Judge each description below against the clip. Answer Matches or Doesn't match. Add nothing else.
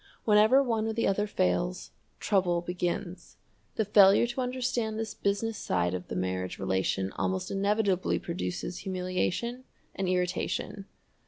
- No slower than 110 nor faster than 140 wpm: Matches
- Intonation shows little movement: Doesn't match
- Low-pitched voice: Doesn't match